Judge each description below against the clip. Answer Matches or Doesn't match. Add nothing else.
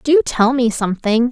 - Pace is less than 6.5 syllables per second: Matches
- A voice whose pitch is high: Matches